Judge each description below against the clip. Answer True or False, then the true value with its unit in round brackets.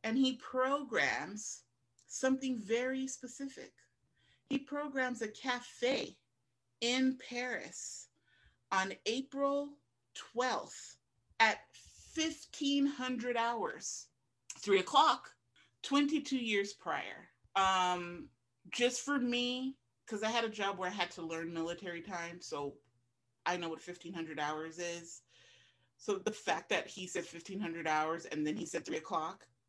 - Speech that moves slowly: True (120 wpm)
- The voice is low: False (210 Hz)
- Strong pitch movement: True (7.7 semitones)